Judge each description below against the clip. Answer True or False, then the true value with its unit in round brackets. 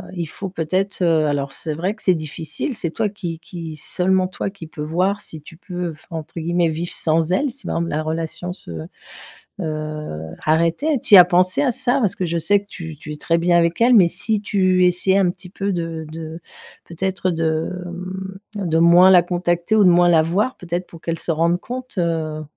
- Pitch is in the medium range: True (175 Hz)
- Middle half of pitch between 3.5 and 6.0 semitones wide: False (2.7 semitones)